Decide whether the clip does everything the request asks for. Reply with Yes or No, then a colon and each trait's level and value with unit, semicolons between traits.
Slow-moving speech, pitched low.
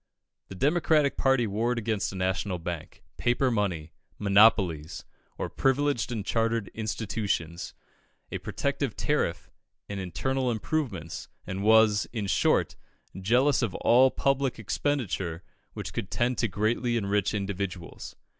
Yes: slow, 125 wpm; low, 110 Hz